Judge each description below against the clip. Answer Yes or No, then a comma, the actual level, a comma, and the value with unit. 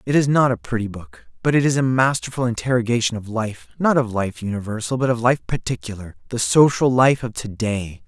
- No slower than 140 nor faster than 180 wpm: No, average, 200 wpm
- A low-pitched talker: Yes, low, 120 Hz